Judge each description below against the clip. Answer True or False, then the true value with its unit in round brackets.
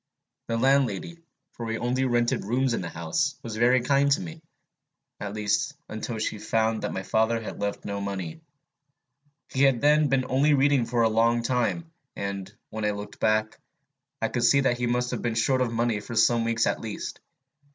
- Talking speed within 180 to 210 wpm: True (195 wpm)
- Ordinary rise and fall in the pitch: True (3.3 semitones)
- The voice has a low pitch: True (115 Hz)